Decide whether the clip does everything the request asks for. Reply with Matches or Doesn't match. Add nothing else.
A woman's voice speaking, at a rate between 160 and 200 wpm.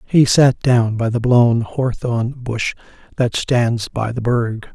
Doesn't match